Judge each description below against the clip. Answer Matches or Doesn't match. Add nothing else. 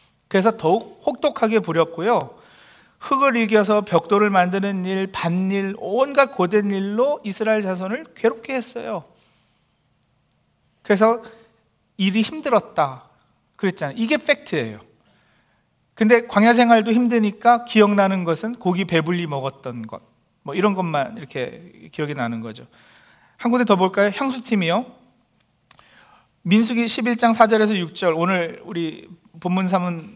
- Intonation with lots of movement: Doesn't match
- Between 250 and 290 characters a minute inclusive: Matches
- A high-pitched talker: Matches